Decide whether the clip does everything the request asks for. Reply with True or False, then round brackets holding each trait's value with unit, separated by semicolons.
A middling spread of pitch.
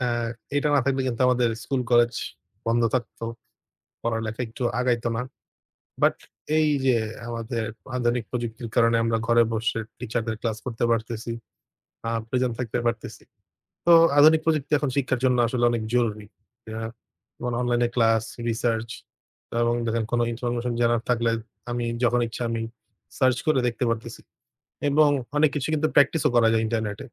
False (1.8 semitones)